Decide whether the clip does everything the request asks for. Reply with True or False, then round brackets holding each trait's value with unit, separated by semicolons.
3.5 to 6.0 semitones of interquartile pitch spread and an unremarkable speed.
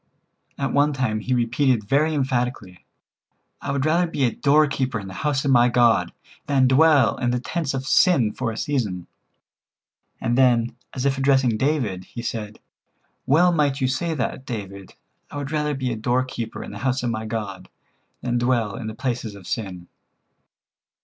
True (3.8 semitones; 175 wpm)